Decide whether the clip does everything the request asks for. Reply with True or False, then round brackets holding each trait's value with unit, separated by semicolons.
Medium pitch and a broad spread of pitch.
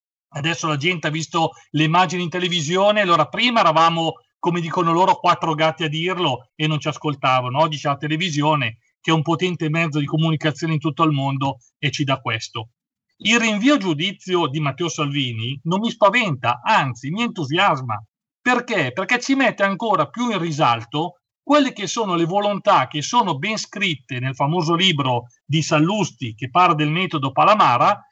False (165 Hz; 3.9 semitones)